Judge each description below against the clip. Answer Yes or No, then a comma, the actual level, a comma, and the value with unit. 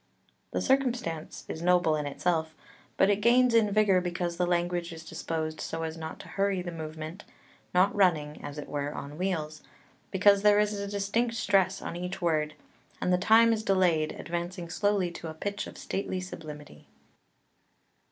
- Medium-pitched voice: Yes, medium, 180 Hz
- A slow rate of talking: No, average, 170 wpm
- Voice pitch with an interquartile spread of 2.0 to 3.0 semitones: No, average, 3.9 semitones